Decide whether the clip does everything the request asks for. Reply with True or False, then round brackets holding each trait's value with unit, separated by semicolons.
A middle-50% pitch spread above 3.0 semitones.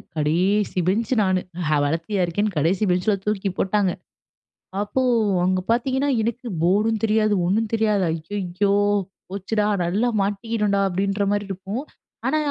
False (2.7 semitones)